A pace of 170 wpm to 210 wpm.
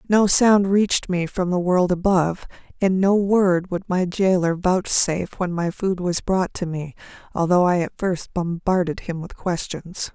Yes: average, 175 wpm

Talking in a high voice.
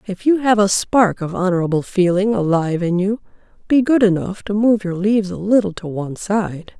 Yes: high, 195 Hz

